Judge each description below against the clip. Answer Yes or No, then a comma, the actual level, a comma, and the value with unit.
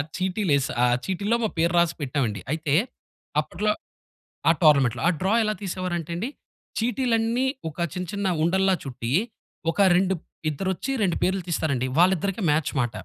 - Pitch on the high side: No, medium, 180 Hz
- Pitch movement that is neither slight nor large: Yes, average, 4.7 semitones